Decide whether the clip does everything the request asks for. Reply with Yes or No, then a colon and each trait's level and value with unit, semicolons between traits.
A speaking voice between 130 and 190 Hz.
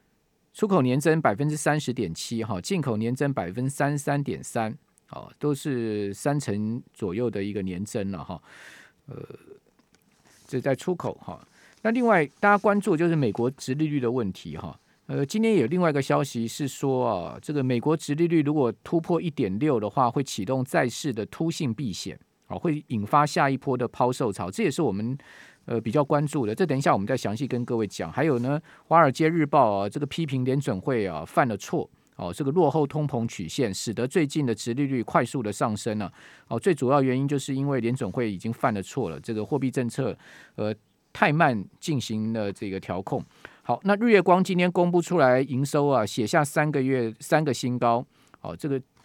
Yes: low, 135 Hz